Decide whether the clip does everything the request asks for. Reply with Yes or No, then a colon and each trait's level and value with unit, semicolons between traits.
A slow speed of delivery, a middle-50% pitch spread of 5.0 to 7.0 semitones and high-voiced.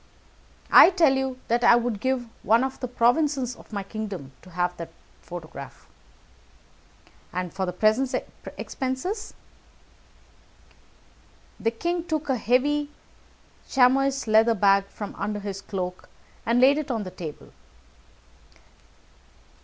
Yes: slow, 120 wpm; average, 5.3 semitones; high, 235 Hz